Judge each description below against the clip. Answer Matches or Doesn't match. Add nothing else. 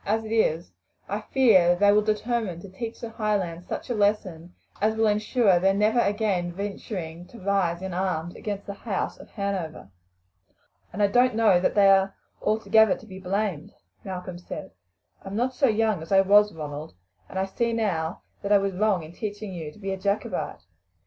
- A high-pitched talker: Matches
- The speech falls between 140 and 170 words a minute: Doesn't match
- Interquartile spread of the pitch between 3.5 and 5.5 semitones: Doesn't match